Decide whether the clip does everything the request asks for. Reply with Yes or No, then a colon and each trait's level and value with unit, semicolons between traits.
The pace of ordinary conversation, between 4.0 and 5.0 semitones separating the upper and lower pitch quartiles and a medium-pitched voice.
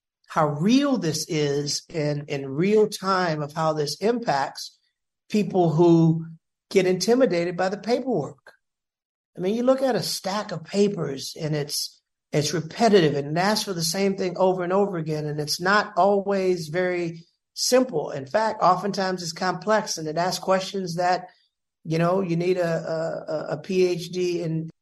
No: average, 165 wpm; average, 3.5 semitones; medium, 180 Hz